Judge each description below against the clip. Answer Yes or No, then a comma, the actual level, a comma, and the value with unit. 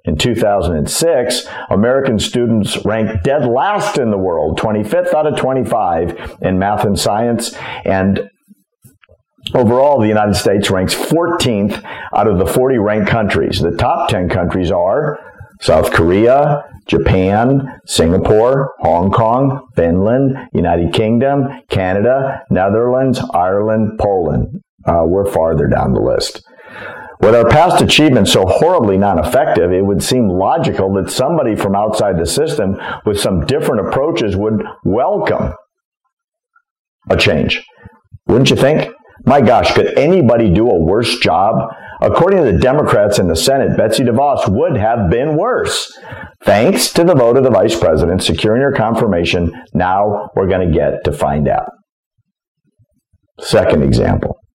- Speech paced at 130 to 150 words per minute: Yes, average, 140 wpm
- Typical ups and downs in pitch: No, wide, 5.7 semitones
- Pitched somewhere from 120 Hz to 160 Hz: No, low, 110 Hz